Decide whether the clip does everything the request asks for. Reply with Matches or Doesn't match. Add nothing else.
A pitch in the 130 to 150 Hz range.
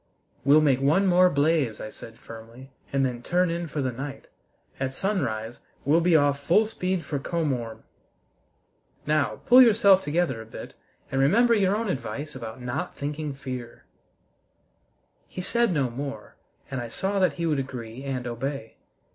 Matches